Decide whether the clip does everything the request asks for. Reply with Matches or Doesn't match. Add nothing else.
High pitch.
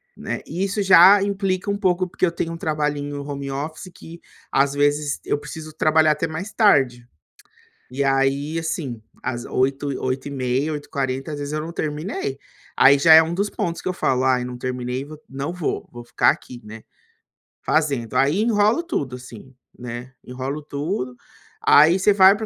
Doesn't match